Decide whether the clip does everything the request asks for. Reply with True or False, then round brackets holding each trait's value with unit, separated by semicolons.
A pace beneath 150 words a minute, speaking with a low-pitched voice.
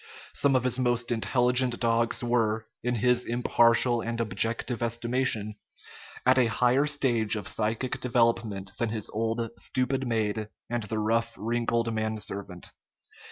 True (140 wpm; 115 Hz)